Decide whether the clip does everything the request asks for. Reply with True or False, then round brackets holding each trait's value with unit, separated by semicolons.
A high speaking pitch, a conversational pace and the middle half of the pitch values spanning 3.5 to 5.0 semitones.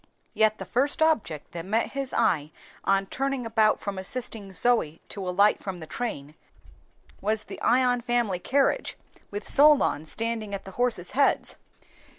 True (220 Hz; 155 wpm; 4.4 semitones)